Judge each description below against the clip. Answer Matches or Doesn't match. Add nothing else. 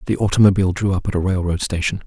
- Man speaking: Matches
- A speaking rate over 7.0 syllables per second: Matches